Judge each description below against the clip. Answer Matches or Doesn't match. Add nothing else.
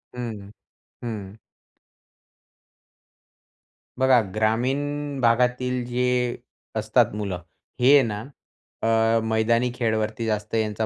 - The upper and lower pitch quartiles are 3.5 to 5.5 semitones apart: Doesn't match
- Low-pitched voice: Matches